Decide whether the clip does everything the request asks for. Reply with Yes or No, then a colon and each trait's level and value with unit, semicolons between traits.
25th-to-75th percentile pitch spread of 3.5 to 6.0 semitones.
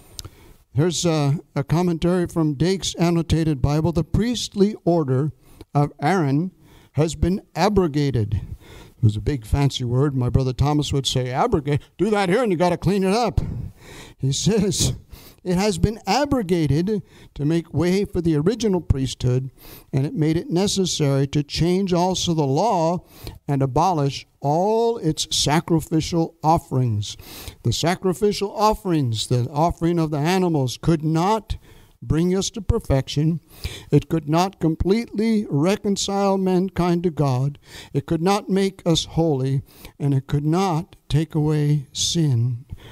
Yes: average, 5.0 semitones